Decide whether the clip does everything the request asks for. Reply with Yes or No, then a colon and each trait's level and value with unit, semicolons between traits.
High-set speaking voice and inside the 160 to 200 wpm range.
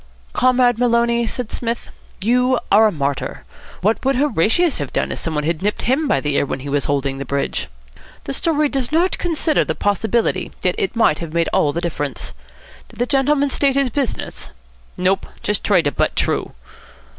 Yes: high, 225 Hz; average, 190 wpm